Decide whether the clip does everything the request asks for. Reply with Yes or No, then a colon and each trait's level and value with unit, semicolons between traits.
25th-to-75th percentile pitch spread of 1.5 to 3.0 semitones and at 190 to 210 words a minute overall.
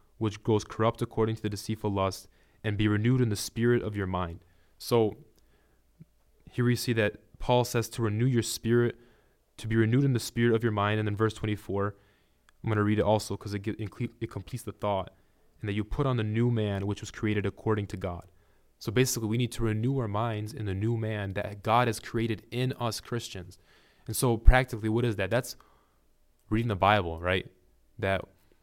Yes: narrow, 2.6 semitones; fast, 205 wpm